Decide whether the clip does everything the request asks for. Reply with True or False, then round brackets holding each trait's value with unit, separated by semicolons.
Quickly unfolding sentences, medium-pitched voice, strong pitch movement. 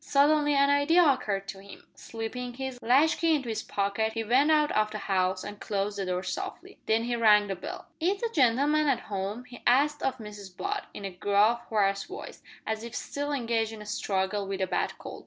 False (210 wpm; 225 Hz; 5.7 semitones)